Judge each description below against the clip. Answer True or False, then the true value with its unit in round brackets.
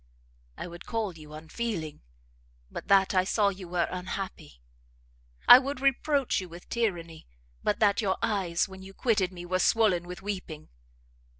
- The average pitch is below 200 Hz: True (190 Hz)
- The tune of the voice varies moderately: True (3.6 semitones)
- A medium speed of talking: True (160 wpm)